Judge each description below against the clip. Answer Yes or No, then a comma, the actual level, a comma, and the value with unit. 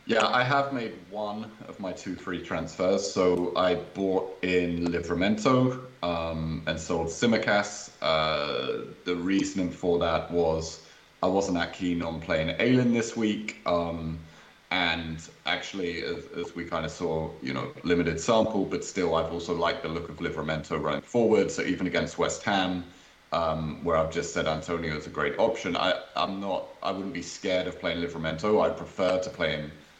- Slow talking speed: No, average, 175 wpm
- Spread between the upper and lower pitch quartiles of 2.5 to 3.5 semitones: Yes, average, 3.2 semitones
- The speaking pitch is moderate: No, very low, 85 Hz